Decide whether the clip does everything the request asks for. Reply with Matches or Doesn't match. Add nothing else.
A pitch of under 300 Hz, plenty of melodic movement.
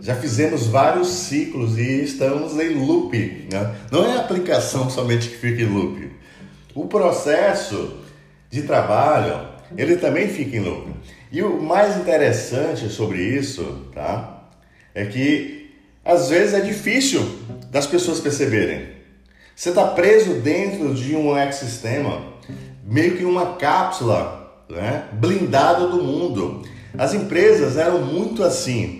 Matches